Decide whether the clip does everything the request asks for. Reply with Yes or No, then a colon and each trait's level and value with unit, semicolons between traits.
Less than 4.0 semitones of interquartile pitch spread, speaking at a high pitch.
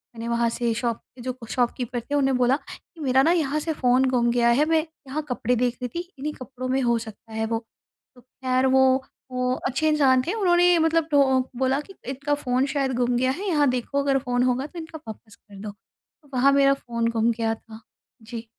Yes: average, 3.1 semitones; very high, 255 Hz